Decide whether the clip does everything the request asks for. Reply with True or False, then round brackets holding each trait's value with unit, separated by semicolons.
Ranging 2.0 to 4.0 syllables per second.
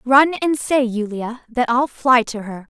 True (3.9 syllables/s)